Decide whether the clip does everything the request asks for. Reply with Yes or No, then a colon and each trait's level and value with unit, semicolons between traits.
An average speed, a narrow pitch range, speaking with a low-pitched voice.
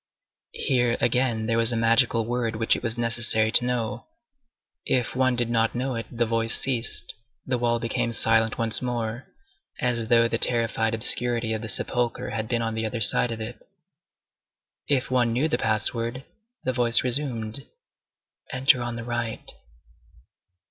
Yes: average, 160 wpm; narrow, 1.4 semitones; low, 115 Hz